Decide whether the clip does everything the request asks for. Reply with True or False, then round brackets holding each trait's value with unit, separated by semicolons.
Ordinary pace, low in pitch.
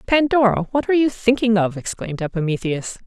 False (155 wpm; 210 Hz)